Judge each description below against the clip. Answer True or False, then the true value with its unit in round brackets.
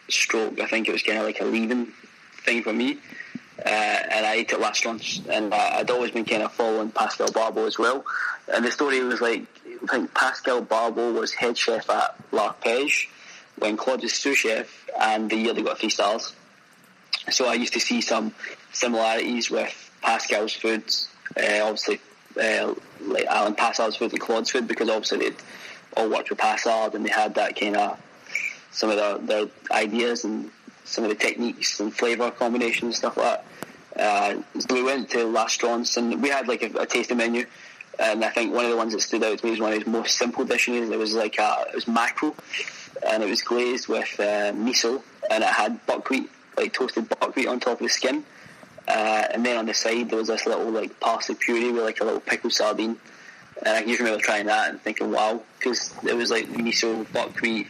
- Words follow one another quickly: True (210 wpm)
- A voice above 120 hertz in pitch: False (115 Hz)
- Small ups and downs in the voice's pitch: True (1.5 semitones)